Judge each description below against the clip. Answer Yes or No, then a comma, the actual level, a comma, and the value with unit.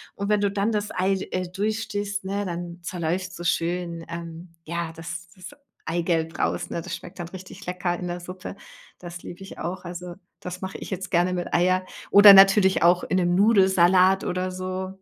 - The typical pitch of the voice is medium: Yes, medium, 180 Hz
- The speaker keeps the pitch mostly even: Yes, narrow, 1.7 semitones